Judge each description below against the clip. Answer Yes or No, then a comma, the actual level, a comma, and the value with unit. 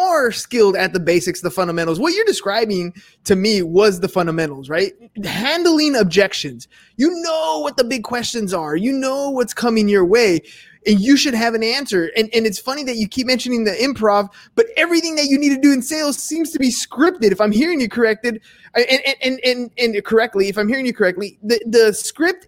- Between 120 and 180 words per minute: No, fast, 205 wpm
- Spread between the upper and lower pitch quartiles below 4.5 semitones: No, average, 5.2 semitones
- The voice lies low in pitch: No, high, 230 Hz